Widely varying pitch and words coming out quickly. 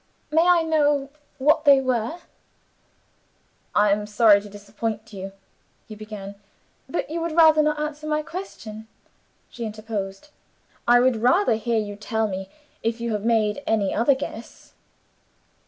No: wide, 6.1 semitones; average, 145 wpm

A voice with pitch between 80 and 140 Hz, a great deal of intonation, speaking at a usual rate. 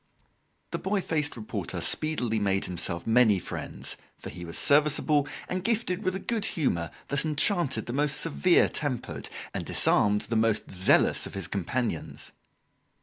Yes: low, 135 Hz; wide, 7.7 semitones; average, 150 wpm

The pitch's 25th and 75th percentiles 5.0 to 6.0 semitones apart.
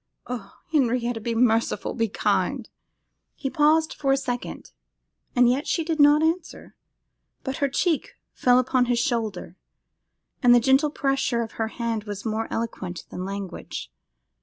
No: average, 3.6 semitones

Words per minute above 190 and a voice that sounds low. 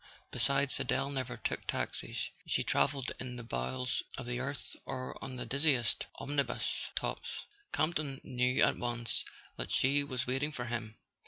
No: average, 155 wpm; low, 130 Hz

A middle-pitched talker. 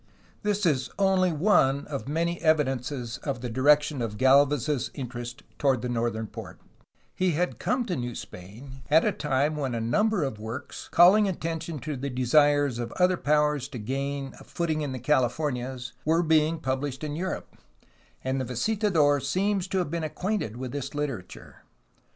Yes: medium, 145 Hz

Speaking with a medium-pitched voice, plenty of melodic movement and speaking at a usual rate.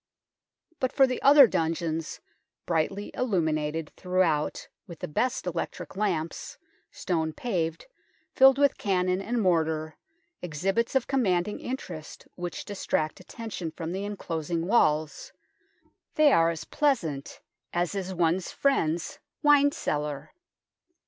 No: medium, 180 Hz; wide, 5.8 semitones; slow, 120 wpm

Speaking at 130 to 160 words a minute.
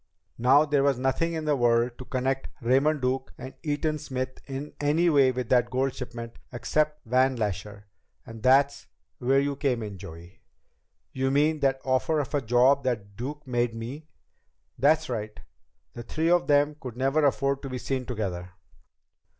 No: average, 170 wpm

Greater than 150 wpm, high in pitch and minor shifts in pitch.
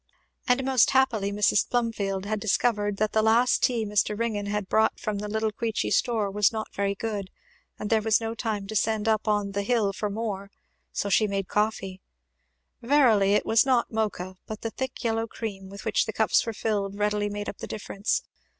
Yes: average, 200 wpm; high, 215 Hz; narrow, 1.9 semitones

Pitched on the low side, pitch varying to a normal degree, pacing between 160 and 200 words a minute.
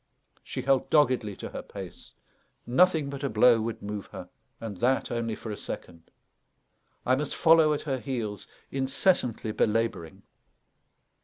No: low, 120 Hz; average, 4.2 semitones; average, 145 wpm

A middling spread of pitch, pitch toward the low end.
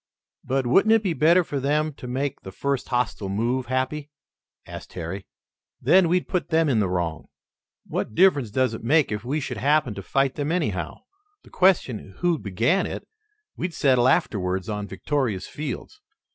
No: wide, 6.4 semitones; low, 130 Hz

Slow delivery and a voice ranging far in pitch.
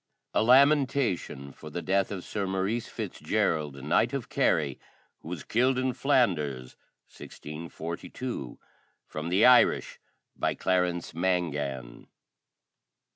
Yes: slow, 115 wpm; wide, 7.6 semitones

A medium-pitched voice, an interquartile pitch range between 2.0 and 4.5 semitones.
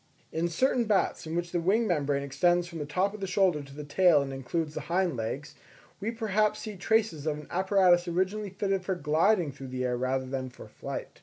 No: medium, 175 Hz; average, 5.2 semitones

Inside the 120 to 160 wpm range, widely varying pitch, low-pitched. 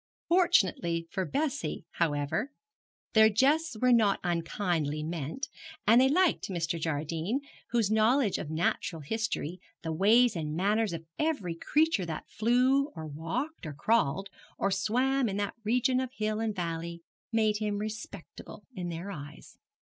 No: average, 145 wpm; wide, 6.4 semitones; high, 205 Hz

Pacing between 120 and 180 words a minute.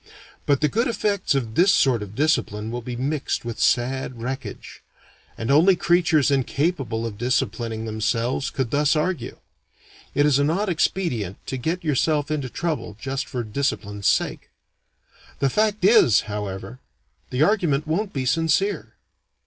Yes: average, 150 wpm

